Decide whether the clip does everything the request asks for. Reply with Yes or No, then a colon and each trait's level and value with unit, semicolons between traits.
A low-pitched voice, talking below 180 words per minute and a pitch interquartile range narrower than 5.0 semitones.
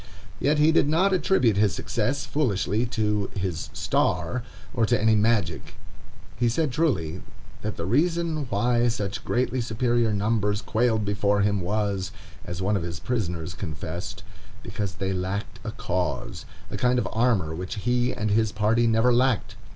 Yes: low, 110 Hz; average, 155 wpm; average, 4.1 semitones